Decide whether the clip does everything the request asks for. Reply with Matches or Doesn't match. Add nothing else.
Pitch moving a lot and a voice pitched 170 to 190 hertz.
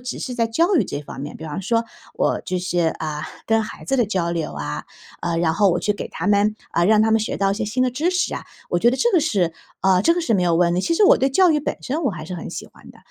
Doesn't match